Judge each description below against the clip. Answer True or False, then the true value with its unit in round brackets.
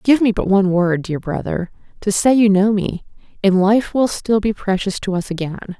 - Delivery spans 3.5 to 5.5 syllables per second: True (5.0 syllables/s)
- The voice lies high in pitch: True (200 Hz)